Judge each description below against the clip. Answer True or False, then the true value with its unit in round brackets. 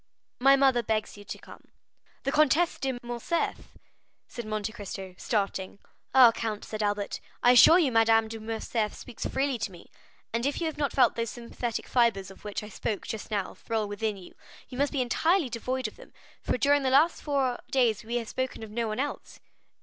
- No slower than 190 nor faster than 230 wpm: True (200 wpm)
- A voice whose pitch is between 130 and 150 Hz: False (235 Hz)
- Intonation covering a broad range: False (3.8 semitones)